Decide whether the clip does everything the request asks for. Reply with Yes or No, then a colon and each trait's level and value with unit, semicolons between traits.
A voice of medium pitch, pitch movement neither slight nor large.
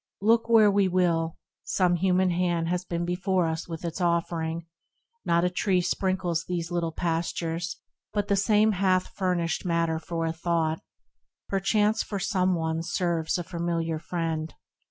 No: medium, 175 Hz; narrow, 2.1 semitones